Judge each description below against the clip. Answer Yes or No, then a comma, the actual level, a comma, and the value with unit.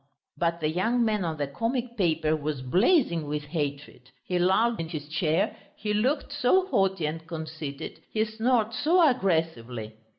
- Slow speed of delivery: No, average, 160 wpm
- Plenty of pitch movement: Yes, wide, 6.8 semitones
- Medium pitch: Yes, medium, 170 Hz